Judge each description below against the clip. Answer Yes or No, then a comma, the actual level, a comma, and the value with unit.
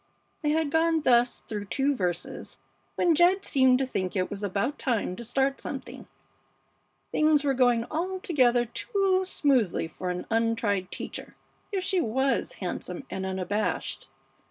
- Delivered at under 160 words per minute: Yes, average, 145 wpm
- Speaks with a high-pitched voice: Yes, very high, 255 Hz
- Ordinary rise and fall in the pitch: No, wide, 7.3 semitones